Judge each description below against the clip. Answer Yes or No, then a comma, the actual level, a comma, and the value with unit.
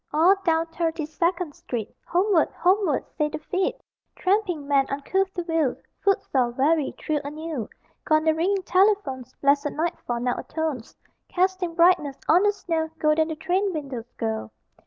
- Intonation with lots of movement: No, average, 4.1 semitones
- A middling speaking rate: Yes, average, 150 wpm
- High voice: Yes, very high, 320 Hz